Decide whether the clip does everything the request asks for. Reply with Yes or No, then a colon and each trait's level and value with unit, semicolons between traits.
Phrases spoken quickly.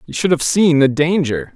Yes: fast, 230 wpm